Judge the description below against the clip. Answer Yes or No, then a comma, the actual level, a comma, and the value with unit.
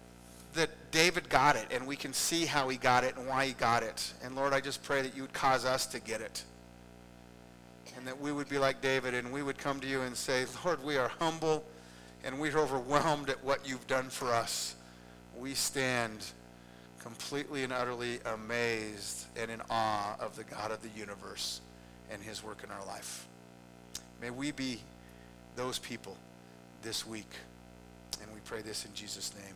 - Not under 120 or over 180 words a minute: No, average, 190 wpm